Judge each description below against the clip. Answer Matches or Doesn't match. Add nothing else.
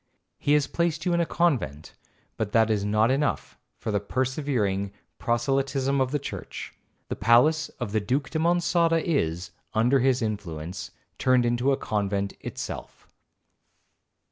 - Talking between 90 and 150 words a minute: Matches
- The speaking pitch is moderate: Doesn't match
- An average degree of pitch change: Doesn't match